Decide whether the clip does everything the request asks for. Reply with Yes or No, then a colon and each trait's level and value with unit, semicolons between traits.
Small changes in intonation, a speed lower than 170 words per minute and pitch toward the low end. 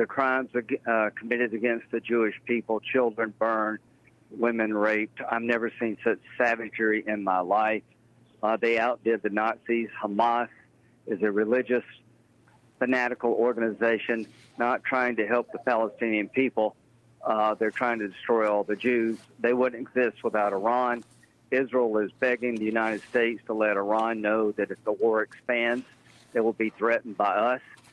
Yes: narrow, 2.0 semitones; average, 155 wpm; low, 115 Hz